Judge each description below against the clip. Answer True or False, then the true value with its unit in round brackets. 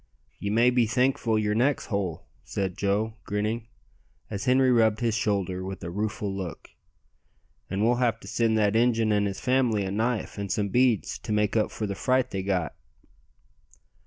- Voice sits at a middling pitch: False (110 Hz)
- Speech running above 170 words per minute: True (180 wpm)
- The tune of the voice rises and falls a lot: False (2.9 semitones)